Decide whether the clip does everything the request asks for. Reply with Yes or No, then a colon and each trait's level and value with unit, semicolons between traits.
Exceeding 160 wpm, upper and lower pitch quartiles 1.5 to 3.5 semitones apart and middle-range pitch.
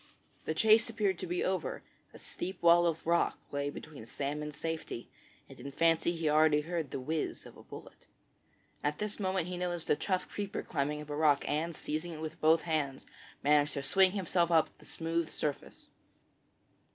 Yes: average, 190 wpm; average, 2.7 semitones; medium, 160 Hz